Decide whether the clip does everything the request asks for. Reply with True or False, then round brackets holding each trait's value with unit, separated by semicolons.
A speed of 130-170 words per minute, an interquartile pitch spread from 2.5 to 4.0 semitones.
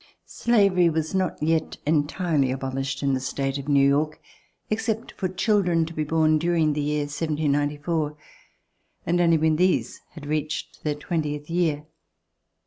True (150 wpm; 2.8 semitones)